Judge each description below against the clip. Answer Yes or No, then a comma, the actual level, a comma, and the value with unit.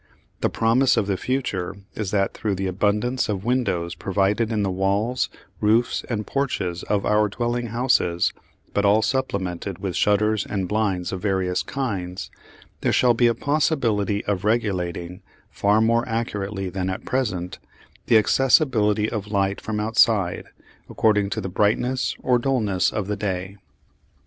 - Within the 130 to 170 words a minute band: Yes, average, 150 wpm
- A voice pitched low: Yes, low, 105 Hz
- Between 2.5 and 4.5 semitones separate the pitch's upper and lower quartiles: Yes, average, 3.3 semitones